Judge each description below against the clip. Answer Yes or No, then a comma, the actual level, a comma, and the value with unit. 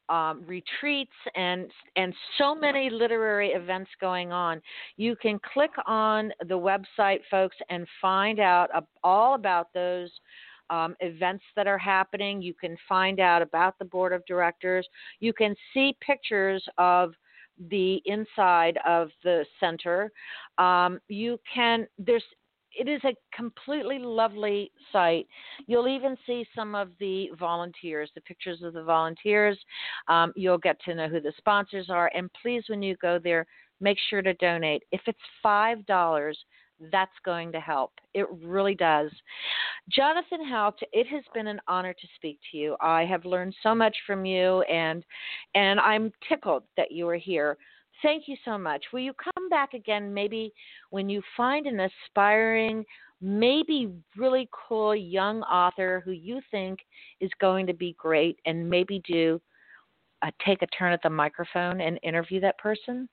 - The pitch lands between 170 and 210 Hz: Yes, high, 190 Hz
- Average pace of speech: Yes, average, 160 wpm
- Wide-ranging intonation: No, average, 4.0 semitones